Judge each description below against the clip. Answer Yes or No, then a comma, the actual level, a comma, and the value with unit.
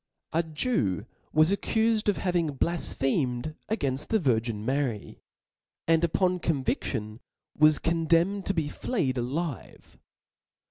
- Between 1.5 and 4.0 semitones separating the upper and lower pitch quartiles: No, average, 5.3 semitones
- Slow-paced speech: Yes, slow, 120 wpm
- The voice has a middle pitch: Yes, medium, 155 Hz